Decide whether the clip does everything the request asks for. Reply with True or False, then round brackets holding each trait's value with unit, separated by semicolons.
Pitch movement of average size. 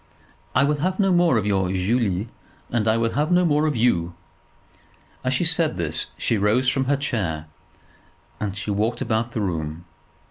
False (6.1 semitones)